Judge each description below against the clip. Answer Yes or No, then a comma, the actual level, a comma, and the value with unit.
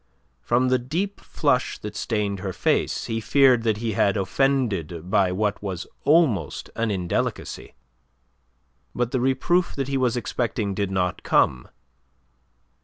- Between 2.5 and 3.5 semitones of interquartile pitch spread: No, average, 4.8 semitones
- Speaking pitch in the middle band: No, low, 115 Hz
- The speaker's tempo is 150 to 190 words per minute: No, average, 140 wpm